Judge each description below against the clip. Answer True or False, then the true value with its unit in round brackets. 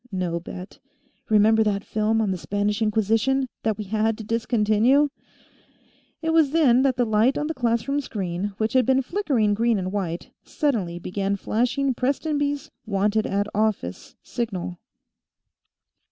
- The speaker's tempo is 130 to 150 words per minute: True (145 wpm)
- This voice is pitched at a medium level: False (220 Hz)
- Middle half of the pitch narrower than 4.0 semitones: False (4.3 semitones)